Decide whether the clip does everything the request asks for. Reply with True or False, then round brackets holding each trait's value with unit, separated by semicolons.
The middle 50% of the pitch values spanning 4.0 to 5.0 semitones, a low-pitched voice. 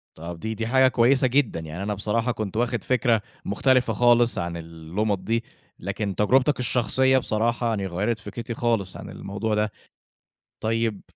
False (3.3 semitones; 110 Hz)